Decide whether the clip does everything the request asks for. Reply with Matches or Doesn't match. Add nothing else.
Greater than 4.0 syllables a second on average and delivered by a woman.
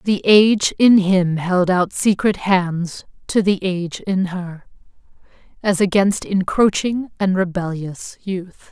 Doesn't match